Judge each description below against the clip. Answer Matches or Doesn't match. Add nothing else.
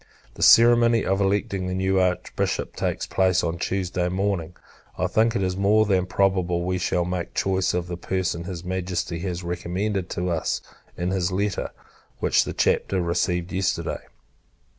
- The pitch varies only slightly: Matches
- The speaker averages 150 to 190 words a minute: Matches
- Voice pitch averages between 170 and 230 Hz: Doesn't match